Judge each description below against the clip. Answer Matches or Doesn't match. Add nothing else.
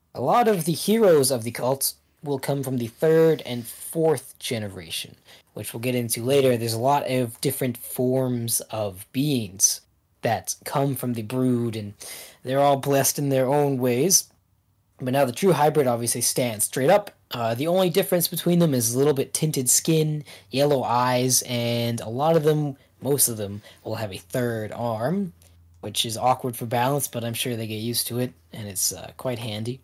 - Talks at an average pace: Matches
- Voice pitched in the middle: Doesn't match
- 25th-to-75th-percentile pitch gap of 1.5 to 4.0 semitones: Matches